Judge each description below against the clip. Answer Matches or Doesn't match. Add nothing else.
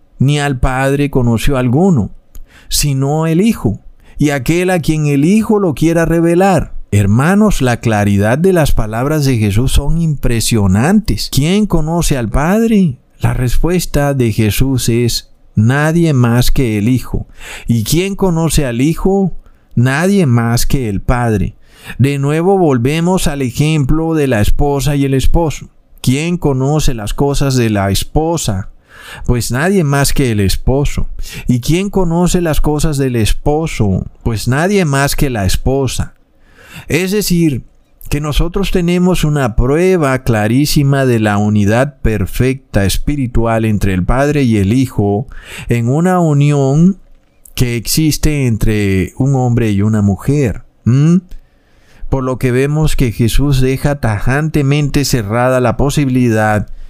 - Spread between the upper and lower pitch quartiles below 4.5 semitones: Doesn't match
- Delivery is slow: Doesn't match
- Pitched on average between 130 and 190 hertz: Matches